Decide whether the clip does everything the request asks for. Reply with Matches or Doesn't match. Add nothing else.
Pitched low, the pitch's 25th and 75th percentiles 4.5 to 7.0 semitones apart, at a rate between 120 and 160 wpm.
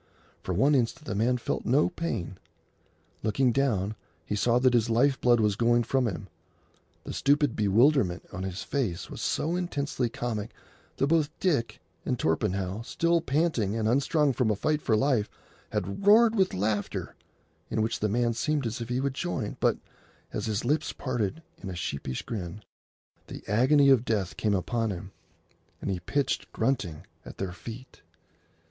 Doesn't match